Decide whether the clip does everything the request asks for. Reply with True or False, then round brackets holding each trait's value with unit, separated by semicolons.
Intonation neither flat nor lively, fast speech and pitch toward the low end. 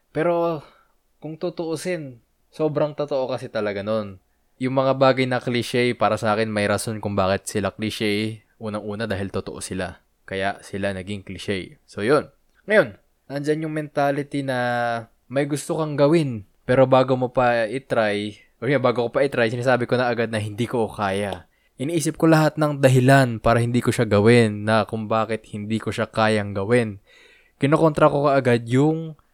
True (4.7 semitones; 170 wpm; 120 Hz)